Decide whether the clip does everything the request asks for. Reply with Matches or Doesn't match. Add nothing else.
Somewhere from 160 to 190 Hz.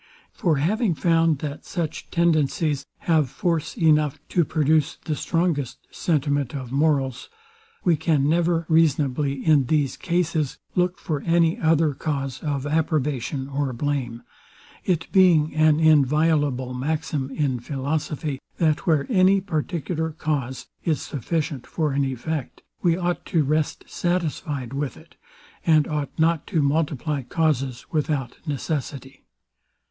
Doesn't match